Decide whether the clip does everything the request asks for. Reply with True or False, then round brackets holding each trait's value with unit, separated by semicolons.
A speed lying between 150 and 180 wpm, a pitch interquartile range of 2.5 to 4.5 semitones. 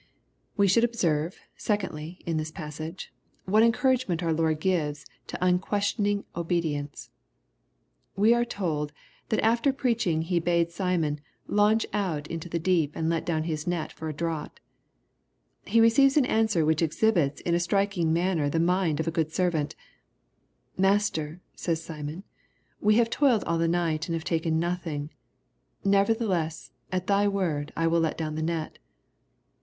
True (160 wpm; 4.1 semitones)